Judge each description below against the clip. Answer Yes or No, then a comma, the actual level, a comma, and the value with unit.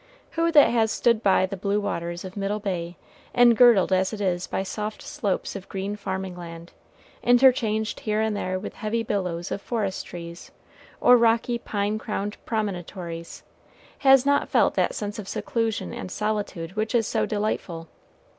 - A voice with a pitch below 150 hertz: No, high, 205 Hz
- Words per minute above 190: No, average, 165 wpm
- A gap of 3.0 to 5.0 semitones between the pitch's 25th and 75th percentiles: Yes, average, 3.3 semitones